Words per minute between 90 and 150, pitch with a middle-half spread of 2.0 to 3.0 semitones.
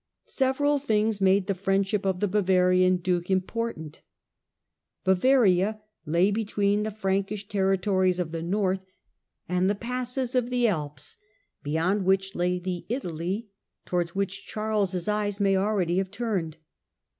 Yes: slow, 135 wpm; average, 2.7 semitones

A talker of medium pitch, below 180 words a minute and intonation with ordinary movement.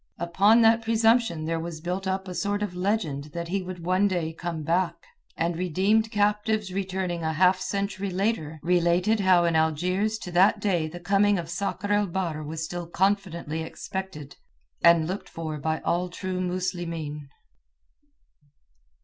Yes: medium, 180 Hz; average, 160 wpm; average, 3.1 semitones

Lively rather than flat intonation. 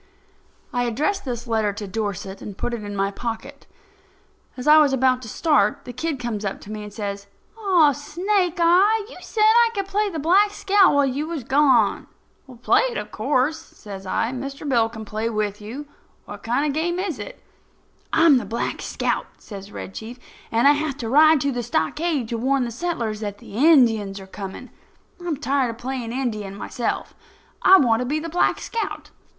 Yes: wide, 6.2 semitones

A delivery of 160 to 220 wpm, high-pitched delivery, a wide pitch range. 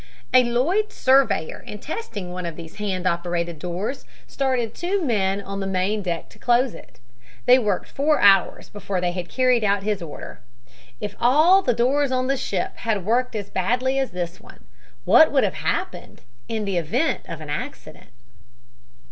Yes: average, 170 wpm; high, 210 Hz; wide, 5.9 semitones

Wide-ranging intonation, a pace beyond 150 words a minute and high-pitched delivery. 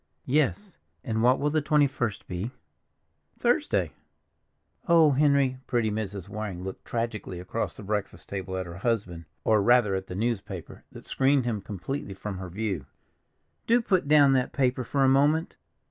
No: wide, 5.8 semitones; average, 160 wpm; low, 115 Hz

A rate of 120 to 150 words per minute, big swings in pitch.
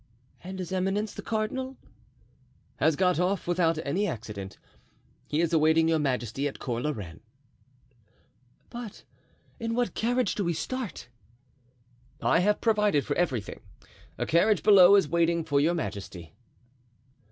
Yes: average, 140 wpm; wide, 6.1 semitones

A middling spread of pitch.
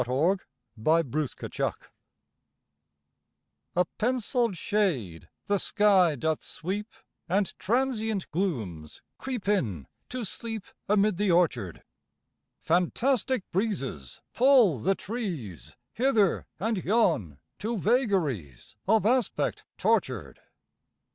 No: wide, 6.5 semitones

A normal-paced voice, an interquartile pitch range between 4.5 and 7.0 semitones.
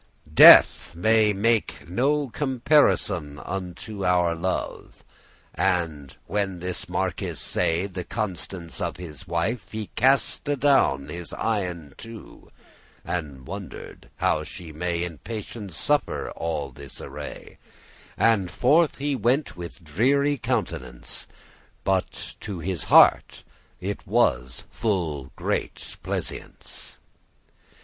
No: slow, 115 wpm; wide, 5.5 semitones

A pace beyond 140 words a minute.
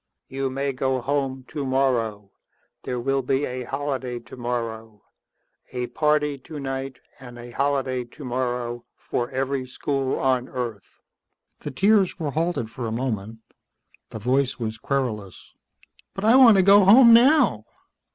No: slow, 135 wpm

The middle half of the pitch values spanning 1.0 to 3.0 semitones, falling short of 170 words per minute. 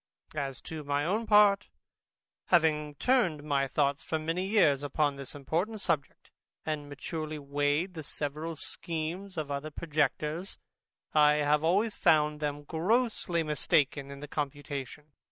Yes: average, 2.7 semitones; slow, 135 wpm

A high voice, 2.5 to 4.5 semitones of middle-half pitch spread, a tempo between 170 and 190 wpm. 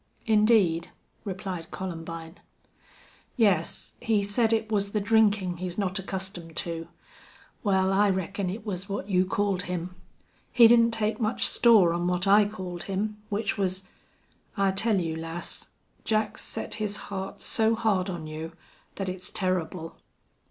No: high, 195 Hz; average, 2.9 semitones; average, 150 wpm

